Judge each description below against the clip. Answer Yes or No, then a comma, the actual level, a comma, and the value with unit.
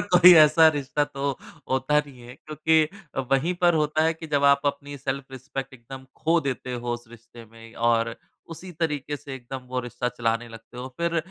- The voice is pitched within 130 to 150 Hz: Yes, low, 135 Hz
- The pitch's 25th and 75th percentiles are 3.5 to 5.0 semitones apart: Yes, average, 4.0 semitones